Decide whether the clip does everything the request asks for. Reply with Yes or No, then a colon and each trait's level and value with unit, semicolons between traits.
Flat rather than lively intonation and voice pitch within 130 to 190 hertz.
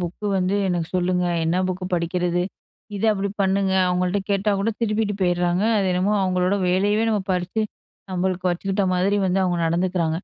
Yes: narrow, 1.8 semitones; medium, 185 Hz